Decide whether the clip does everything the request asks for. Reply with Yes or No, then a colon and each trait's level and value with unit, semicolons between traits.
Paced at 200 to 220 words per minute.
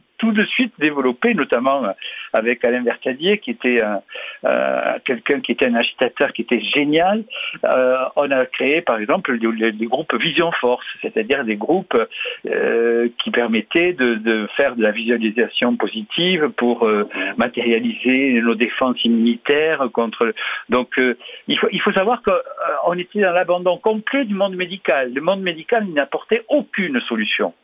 No: average, 155 wpm